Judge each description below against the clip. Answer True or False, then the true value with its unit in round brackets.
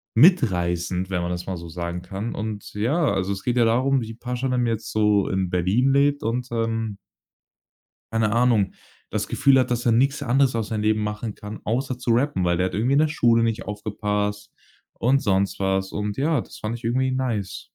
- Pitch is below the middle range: True (110 Hz)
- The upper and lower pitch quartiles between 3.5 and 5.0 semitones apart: True (4.0 semitones)